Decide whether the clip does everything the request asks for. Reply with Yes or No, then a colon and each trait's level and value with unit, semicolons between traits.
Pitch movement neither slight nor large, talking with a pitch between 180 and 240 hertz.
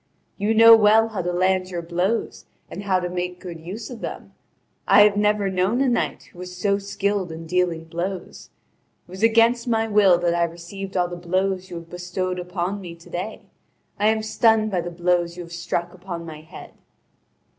Yes: average, 3.0 semitones; medium, 185 Hz